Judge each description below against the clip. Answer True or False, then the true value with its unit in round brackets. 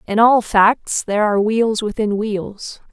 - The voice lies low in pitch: False (215 Hz)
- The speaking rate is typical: True (165 wpm)